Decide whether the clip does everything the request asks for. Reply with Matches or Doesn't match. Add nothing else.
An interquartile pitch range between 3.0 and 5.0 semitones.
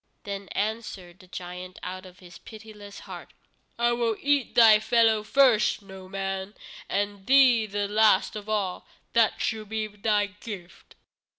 Doesn't match